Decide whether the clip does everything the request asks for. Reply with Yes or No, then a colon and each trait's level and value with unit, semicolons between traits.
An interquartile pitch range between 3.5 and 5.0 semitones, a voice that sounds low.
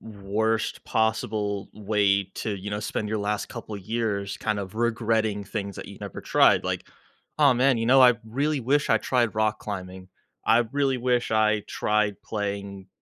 No: narrow, 2.4 semitones; low, 110 Hz